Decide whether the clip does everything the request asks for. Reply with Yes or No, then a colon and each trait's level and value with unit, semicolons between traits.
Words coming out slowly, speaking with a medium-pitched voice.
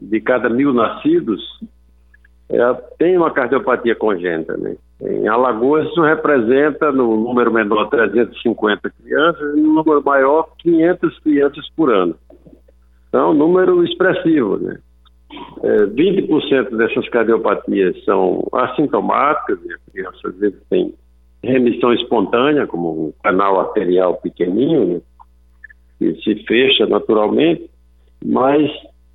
Yes: slow, 110 wpm; medium, 145 Hz